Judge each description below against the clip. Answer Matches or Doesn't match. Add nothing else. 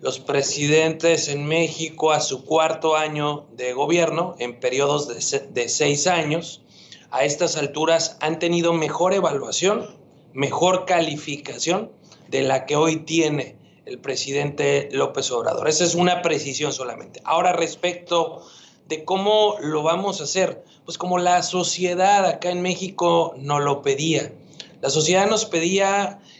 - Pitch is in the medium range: Matches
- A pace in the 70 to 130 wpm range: Doesn't match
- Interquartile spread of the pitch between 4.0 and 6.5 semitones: Doesn't match